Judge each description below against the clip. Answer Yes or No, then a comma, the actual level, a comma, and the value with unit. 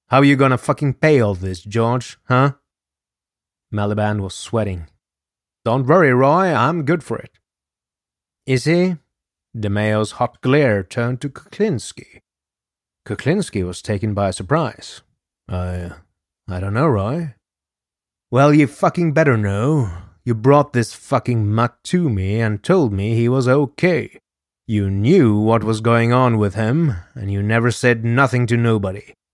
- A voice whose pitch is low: Yes, low, 115 Hz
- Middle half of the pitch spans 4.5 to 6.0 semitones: Yes, wide, 5.5 semitones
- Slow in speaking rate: No, average, 145 wpm